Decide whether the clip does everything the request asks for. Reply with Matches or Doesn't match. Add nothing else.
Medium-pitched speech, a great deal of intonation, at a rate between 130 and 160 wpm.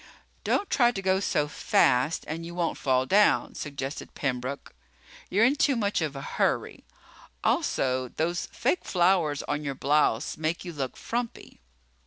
Matches